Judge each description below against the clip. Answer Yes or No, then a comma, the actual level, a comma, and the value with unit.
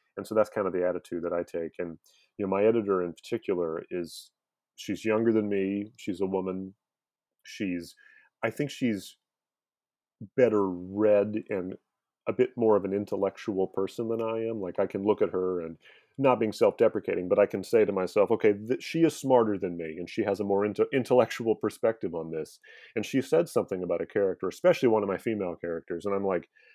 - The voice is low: Yes, low, 100 Hz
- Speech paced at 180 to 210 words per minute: Yes, fast, 205 wpm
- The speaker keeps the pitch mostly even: No, average, 4.3 semitones